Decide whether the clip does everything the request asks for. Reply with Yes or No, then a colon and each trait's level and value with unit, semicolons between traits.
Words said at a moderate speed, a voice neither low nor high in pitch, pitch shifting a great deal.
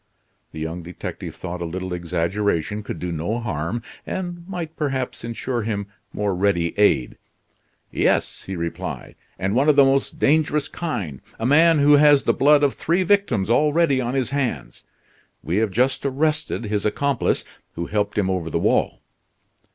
No: average, 165 wpm; low, 115 Hz; wide, 7.7 semitones